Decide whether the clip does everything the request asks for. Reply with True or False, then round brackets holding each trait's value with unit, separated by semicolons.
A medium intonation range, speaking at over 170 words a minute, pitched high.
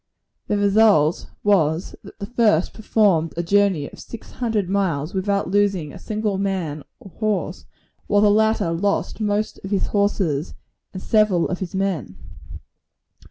False (3.4 semitones; 150 wpm; 200 Hz)